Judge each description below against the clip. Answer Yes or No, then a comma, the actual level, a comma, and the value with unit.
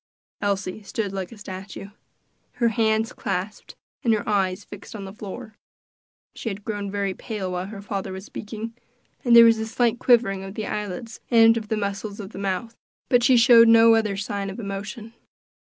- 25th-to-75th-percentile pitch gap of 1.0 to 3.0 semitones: Yes, narrow, 2.5 semitones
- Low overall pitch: No, high, 210 Hz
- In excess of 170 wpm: Yes, average, 185 wpm